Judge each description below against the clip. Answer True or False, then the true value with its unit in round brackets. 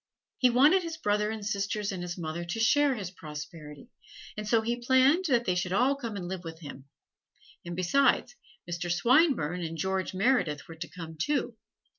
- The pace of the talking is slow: False (185 wpm)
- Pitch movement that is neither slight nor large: False (6.3 semitones)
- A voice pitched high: True (200 Hz)